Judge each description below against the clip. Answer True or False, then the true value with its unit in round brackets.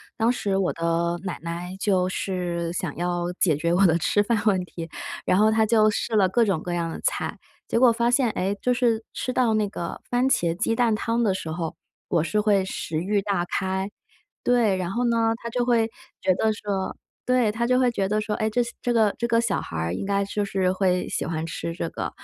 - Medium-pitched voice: False (200 Hz)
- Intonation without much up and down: False (4.4 semitones)